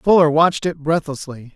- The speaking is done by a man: Yes, male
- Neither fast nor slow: Yes, average, 155 wpm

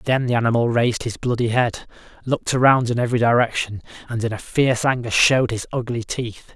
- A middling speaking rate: Yes, average, 185 wpm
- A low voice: Yes, low, 120 Hz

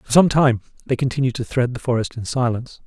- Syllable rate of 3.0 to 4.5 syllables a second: No, 6.2 syllables/s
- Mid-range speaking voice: No, low, 125 Hz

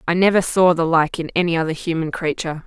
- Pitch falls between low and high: Yes, medium, 170 Hz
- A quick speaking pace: Yes, fast, 225 wpm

